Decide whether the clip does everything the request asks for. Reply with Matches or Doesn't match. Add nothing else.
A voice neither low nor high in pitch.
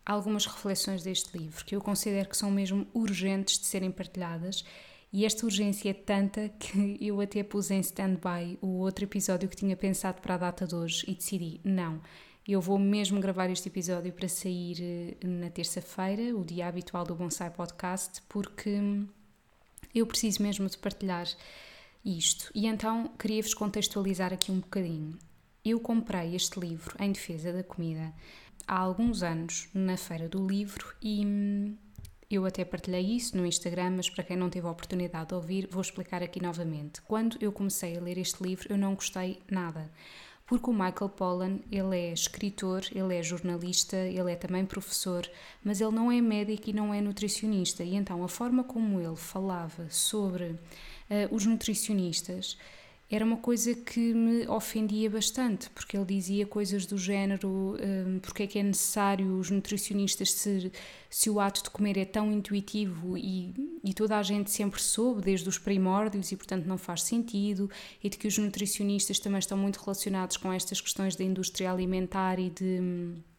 Doesn't match